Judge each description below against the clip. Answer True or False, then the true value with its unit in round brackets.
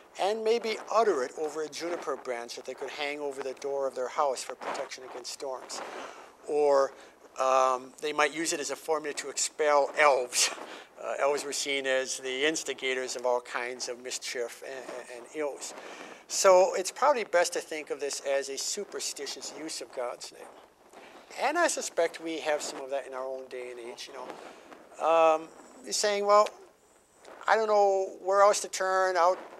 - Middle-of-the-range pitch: True (150 Hz)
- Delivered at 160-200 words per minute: True (190 wpm)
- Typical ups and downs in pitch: False (6.2 semitones)